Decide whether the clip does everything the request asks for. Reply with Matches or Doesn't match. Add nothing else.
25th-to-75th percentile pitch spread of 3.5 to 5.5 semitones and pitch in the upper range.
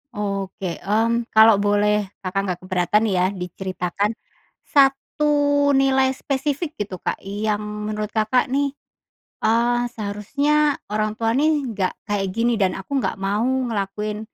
Matches